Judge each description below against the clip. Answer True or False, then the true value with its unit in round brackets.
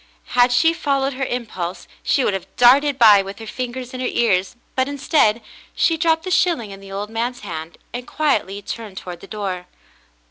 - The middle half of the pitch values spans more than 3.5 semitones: True (5.3 semitones)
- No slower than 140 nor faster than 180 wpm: False (190 wpm)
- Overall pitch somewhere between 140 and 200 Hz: False (240 Hz)